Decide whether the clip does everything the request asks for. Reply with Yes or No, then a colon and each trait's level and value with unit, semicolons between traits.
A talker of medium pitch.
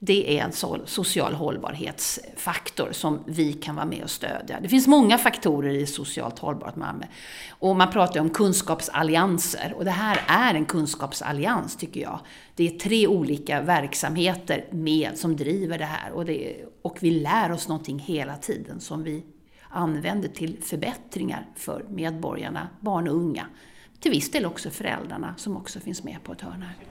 Yes: medium, 165 Hz